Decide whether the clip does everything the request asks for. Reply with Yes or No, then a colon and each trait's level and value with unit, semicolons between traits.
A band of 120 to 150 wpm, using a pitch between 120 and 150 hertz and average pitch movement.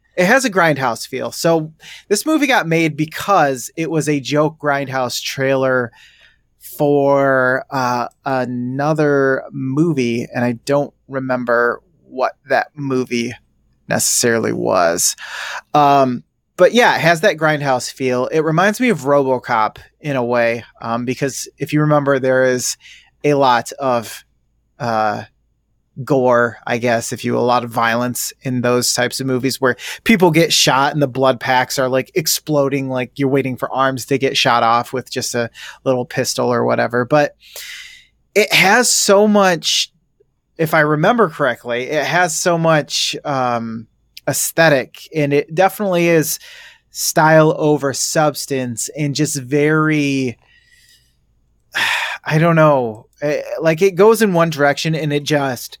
Yes: average, 145 wpm; medium, 140 Hz; average, 4.0 semitones